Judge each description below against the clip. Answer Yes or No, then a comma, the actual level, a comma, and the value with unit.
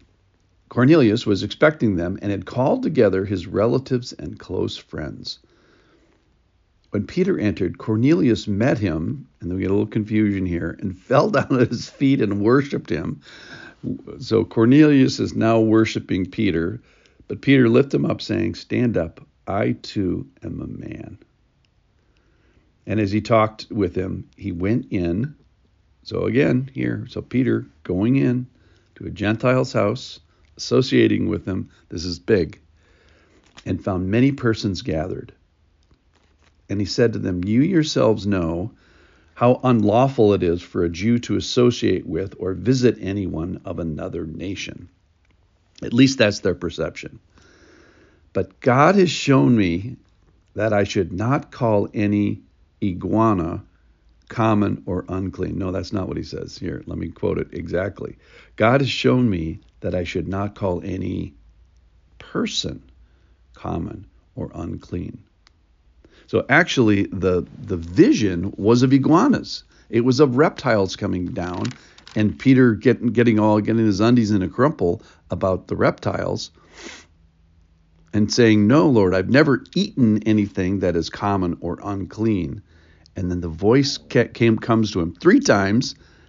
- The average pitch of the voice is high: No, low, 100 Hz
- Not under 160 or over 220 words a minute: No, average, 145 wpm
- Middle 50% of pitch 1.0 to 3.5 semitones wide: No, average, 4.8 semitones